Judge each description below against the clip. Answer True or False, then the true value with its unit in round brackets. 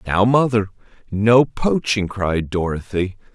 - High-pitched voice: False (105 Hz)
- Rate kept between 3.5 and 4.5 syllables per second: True (3.8 syllables/s)